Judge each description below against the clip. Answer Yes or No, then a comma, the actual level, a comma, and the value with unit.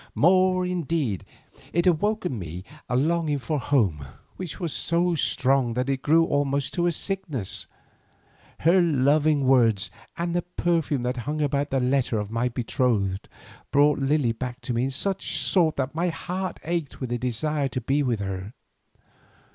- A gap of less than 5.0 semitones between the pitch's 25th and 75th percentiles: No, average, 5.3 semitones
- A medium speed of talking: Yes, average, 165 wpm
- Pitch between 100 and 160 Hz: Yes, medium, 140 Hz